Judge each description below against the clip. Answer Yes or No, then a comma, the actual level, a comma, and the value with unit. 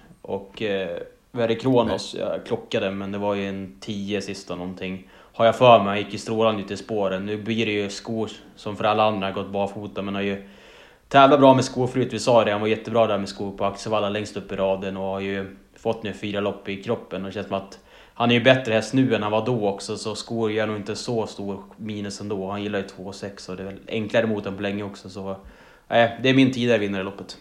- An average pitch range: No, narrow, 2.3 semitones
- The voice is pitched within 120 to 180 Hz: No, low, 105 Hz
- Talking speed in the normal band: No, fast, 260 wpm